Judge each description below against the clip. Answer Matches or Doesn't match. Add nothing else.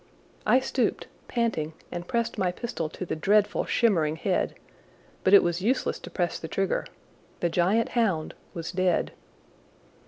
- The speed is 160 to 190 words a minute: Doesn't match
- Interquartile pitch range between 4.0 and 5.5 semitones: Matches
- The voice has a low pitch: Doesn't match